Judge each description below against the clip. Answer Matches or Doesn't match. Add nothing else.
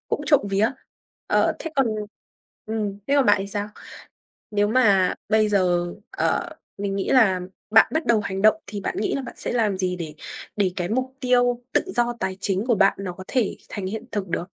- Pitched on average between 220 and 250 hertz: Doesn't match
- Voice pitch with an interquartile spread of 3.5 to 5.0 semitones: Matches